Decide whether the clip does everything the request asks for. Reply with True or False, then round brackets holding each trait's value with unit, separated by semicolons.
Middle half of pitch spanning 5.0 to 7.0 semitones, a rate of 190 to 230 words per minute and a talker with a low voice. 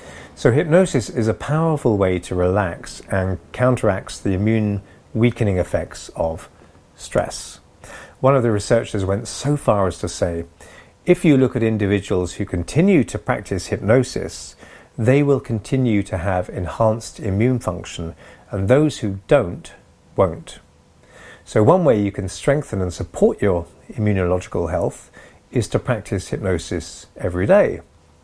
False (5.3 semitones; 140 wpm; 105 Hz)